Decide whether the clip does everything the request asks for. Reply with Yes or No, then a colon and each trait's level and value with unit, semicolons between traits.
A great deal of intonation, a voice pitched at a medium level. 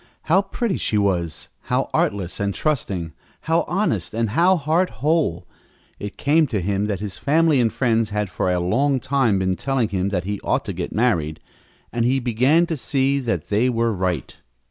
No: wide, 6.2 semitones; low, 115 Hz